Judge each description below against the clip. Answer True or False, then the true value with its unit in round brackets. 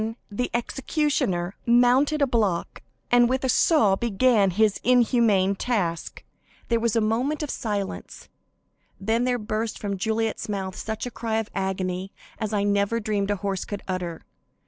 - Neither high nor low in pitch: False (220 Hz)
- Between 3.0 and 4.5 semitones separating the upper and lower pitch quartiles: True (3.5 semitones)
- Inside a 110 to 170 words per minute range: True (160 wpm)